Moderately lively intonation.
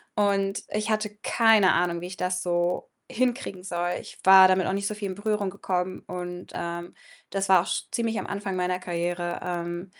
No: narrow, 2.3 semitones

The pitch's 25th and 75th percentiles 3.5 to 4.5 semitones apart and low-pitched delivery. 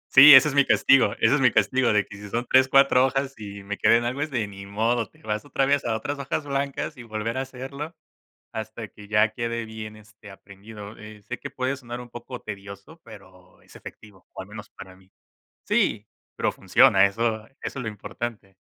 Yes: average, 4.1 semitones; low, 115 Hz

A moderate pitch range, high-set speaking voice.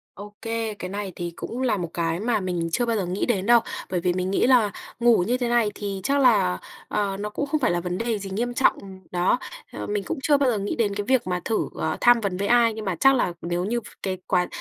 Yes: average, 4.6 semitones; high, 205 Hz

